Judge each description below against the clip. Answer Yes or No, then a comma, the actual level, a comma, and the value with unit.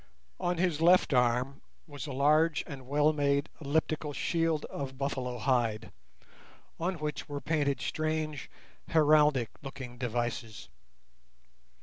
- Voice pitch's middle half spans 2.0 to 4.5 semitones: Yes, average, 3.3 semitones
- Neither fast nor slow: No, slow, 115 wpm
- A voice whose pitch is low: No, medium, 145 Hz